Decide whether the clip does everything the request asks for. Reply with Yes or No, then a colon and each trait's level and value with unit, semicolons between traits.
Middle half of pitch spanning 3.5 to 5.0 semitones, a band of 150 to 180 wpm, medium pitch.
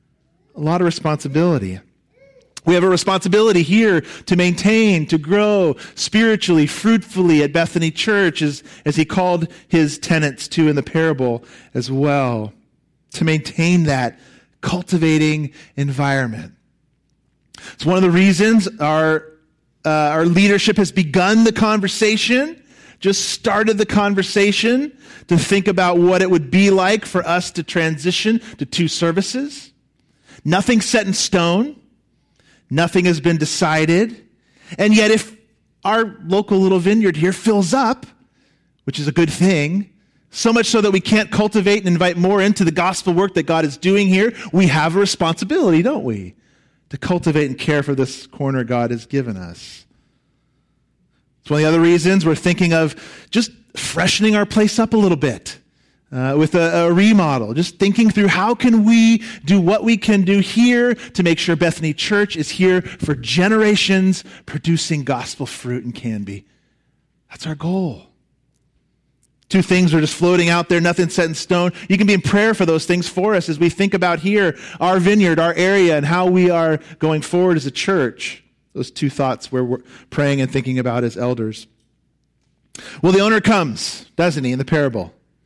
Yes: average, 4.7 semitones; average, 165 wpm; medium, 175 Hz